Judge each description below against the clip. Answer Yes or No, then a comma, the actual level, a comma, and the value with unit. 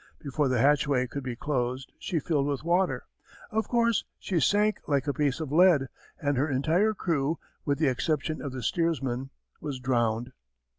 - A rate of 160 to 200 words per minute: Yes, average, 175 wpm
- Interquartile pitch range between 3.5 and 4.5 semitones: Yes, average, 4.0 semitones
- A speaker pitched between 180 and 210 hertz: No, medium, 145 Hz